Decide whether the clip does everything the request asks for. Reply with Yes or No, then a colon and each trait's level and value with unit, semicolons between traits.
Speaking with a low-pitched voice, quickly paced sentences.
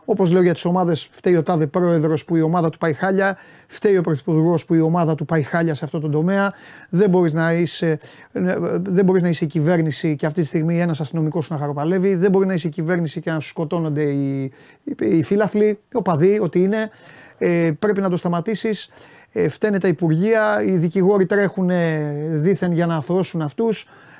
No: medium, 175 Hz; fast, 190 wpm